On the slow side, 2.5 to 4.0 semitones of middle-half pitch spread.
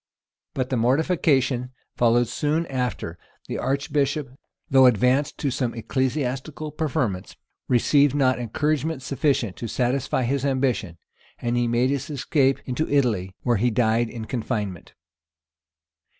Yes: slow, 120 wpm; average, 2.9 semitones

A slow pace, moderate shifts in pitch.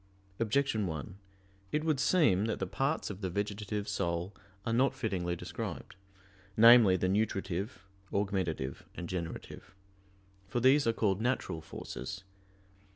Yes: slow, 130 wpm; average, 4.0 semitones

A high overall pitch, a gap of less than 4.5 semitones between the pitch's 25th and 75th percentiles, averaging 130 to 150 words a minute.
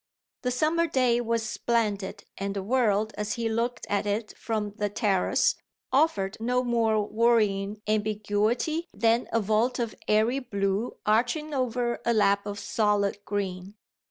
Yes: high, 220 Hz; average, 2.8 semitones; average, 145 wpm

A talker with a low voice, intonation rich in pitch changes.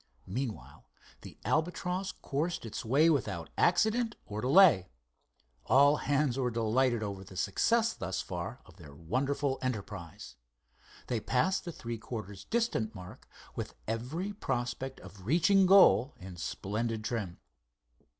Yes: low, 125 Hz; wide, 7.5 semitones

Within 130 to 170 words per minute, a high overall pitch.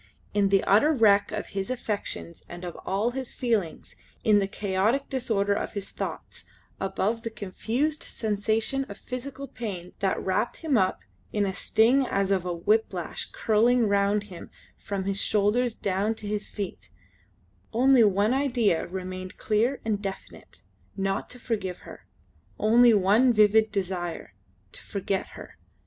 Yes: average, 150 wpm; high, 210 Hz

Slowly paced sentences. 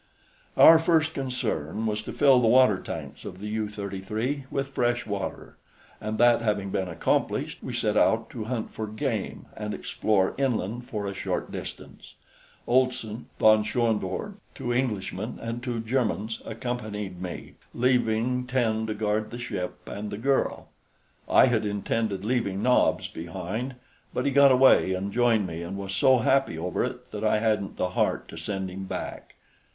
No: average, 165 wpm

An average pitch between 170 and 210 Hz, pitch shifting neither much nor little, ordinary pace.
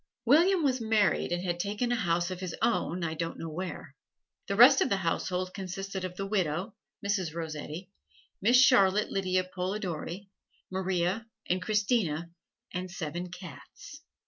Yes: medium, 185 Hz; average, 3.0 semitones; average, 150 wpm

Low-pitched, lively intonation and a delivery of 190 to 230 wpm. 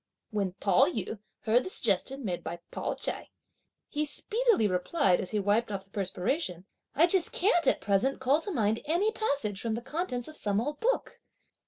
No: high, 235 Hz; wide, 7.7 semitones; average, 195 wpm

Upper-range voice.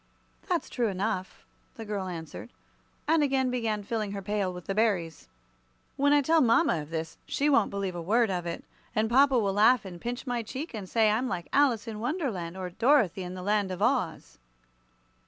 Yes: high, 215 Hz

